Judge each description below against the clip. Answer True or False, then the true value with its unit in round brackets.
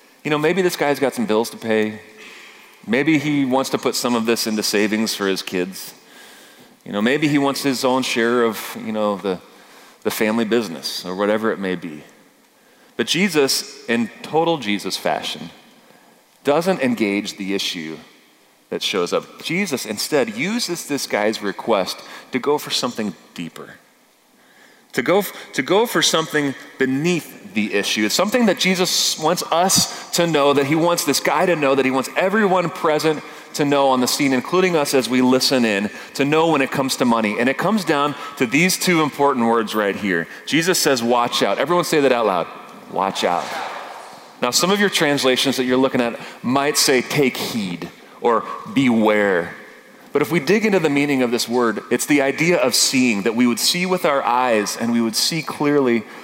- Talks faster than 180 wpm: True (190 wpm)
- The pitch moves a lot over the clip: True (5.7 semitones)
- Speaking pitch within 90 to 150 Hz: True (135 Hz)